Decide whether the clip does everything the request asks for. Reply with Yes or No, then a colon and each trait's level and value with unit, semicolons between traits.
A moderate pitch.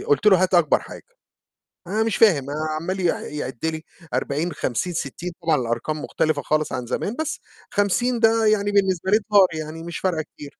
Yes: medium, 175 Hz